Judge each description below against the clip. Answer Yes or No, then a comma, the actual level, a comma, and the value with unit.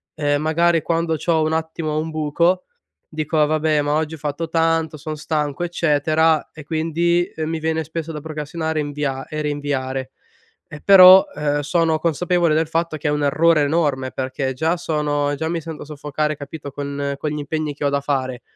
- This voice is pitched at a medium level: Yes, medium, 155 Hz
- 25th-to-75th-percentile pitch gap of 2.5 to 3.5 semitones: No, narrow, 1.8 semitones